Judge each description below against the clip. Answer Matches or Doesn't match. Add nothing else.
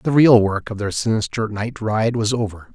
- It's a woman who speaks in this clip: Doesn't match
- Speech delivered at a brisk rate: Matches